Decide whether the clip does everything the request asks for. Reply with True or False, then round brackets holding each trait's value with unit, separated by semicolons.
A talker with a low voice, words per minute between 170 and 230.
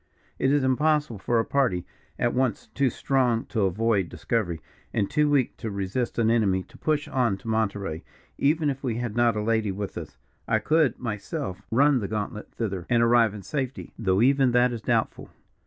True (115 Hz; 190 wpm)